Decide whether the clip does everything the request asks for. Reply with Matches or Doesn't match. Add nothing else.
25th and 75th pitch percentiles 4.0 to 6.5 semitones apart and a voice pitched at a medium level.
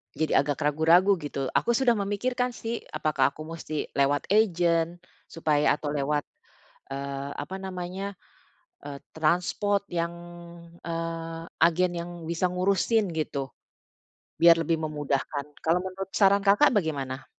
Matches